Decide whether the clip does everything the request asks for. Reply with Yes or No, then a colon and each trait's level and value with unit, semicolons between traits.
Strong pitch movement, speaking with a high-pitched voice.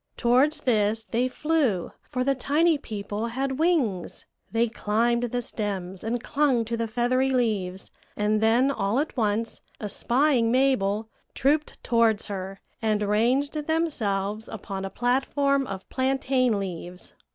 No: average, 4.4 semitones; high, 235 Hz